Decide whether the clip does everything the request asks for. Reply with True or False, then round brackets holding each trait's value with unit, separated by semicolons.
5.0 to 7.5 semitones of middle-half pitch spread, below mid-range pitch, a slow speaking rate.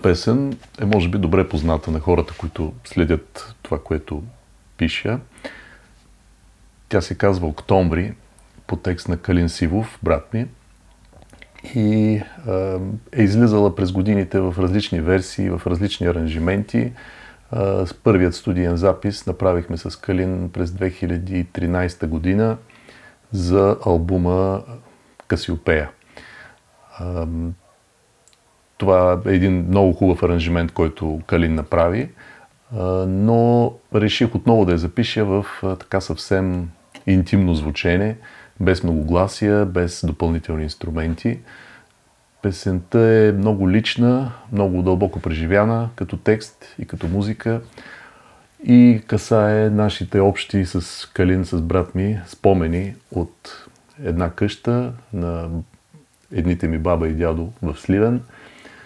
False (3.5 semitones; 95 Hz; 110 wpm)